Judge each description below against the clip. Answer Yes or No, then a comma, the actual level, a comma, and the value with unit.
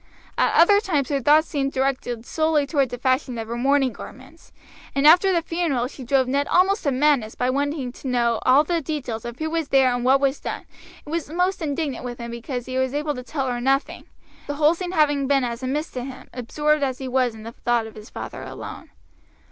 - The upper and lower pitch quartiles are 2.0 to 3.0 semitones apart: No, average, 3.4 semitones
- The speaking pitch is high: Yes, very high, 275 Hz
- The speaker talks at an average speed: No, fast, 230 wpm